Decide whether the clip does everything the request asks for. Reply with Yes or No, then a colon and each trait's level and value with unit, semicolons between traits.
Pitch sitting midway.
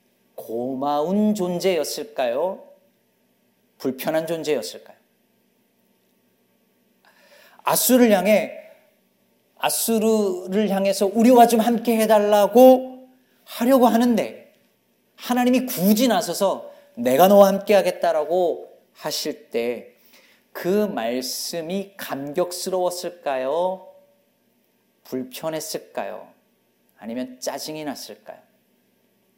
No: high, 200 Hz